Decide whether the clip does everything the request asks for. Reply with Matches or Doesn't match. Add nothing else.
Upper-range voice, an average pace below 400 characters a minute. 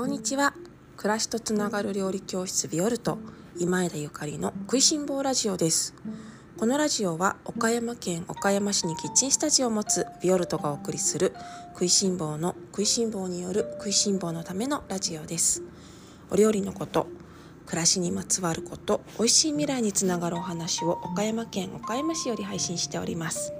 Matches